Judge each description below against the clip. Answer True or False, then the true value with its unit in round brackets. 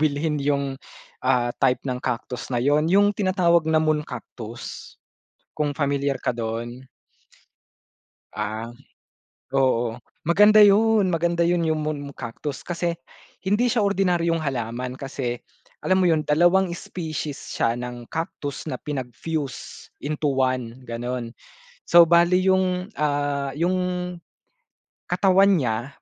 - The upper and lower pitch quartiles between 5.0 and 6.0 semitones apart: True (5.3 semitones)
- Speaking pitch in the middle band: True (150 Hz)